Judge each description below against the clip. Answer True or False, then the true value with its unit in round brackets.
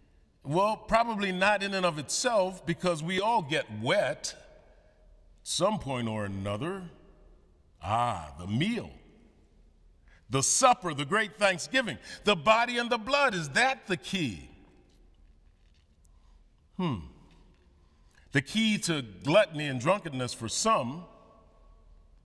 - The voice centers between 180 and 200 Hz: False (135 Hz)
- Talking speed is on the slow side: True (115 wpm)